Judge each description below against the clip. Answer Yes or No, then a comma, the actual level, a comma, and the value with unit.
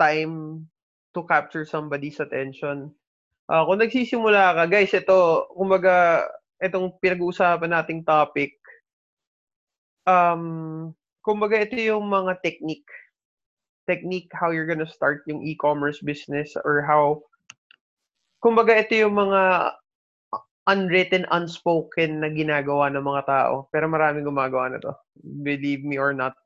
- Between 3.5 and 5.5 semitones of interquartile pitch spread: Yes, average, 4.1 semitones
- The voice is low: No, medium, 165 Hz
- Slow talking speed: Yes, slow, 120 wpm